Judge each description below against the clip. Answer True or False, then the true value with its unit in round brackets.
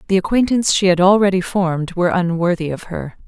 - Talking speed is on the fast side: False (185 wpm)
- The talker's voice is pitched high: False (180 Hz)